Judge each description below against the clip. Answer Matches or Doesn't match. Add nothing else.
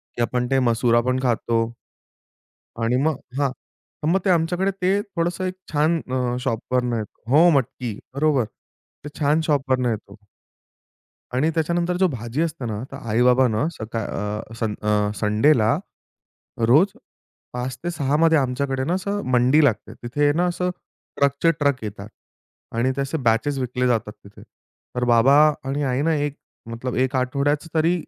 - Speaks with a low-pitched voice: Matches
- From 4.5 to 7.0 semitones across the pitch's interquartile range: Matches